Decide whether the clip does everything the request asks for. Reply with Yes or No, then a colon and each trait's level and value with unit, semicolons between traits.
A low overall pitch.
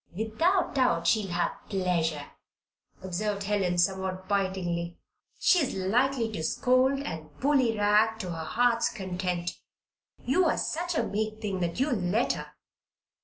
No: high, 205 Hz